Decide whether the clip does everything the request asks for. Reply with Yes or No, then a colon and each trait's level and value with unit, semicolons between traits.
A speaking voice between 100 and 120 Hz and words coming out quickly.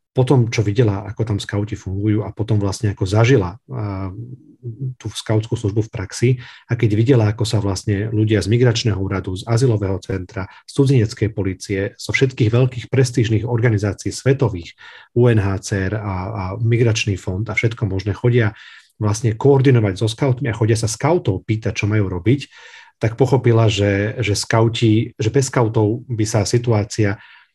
No: low, 110 Hz; average, 155 wpm